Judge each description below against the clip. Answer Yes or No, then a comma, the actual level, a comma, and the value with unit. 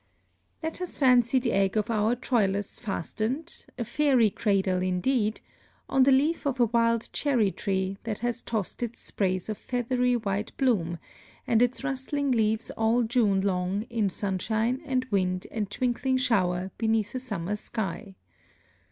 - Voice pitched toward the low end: No, high, 225 Hz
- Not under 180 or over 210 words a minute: No, average, 150 wpm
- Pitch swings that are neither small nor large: Yes, average, 4.2 semitones